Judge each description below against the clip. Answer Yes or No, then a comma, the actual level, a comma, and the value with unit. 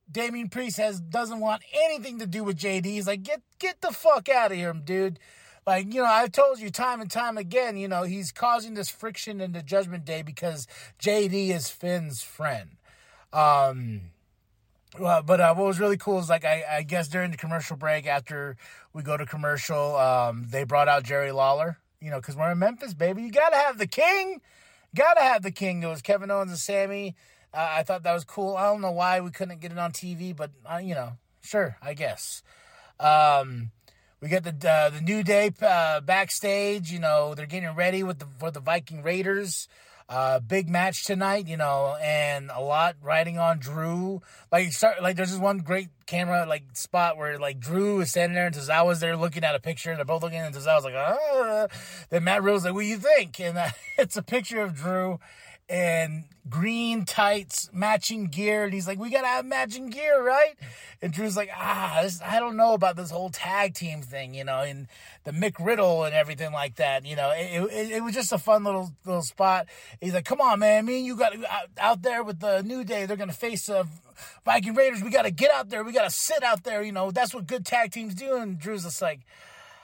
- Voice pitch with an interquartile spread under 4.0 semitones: No, average, 4.8 semitones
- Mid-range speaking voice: Yes, medium, 180 Hz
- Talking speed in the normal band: No, fast, 220 wpm